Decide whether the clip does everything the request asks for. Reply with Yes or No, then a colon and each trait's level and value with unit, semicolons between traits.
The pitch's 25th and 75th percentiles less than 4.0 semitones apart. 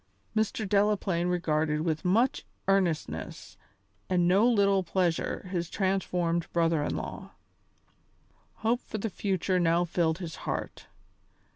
Yes: average, 2.9 semitones